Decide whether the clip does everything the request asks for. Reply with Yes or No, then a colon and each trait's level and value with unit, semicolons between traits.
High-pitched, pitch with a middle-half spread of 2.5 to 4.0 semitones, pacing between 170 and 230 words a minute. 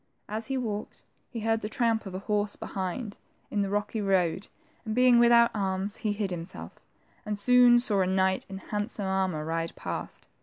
Yes: high, 205 Hz; average, 2.9 semitones; average, 185 wpm